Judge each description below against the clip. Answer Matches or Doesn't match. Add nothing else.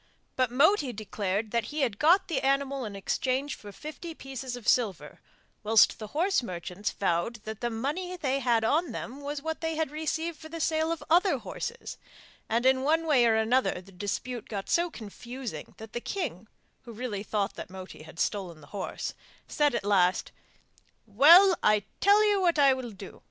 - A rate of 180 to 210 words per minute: Matches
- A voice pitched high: Matches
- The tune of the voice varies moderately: Doesn't match